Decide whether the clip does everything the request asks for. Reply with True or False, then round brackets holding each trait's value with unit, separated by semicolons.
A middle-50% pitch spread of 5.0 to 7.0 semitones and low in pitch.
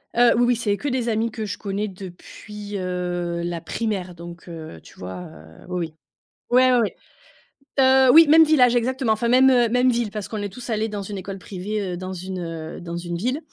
False (5.4 semitones; 205 Hz)